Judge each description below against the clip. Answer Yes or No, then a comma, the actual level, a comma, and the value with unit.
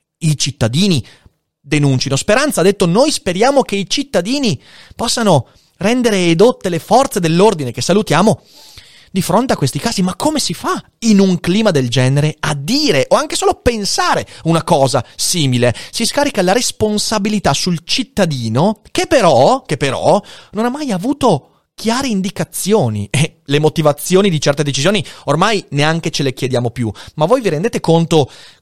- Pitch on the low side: No, medium, 185 Hz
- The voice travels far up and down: Yes, wide, 7.2 semitones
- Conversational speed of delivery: Yes, average, 160 wpm